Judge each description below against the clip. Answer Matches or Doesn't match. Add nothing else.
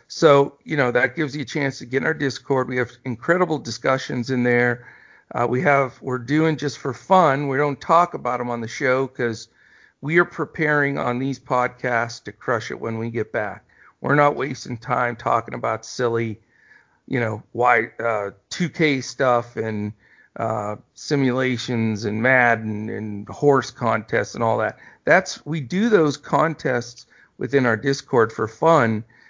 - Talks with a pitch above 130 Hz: Doesn't match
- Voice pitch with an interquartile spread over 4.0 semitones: Doesn't match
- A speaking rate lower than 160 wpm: Doesn't match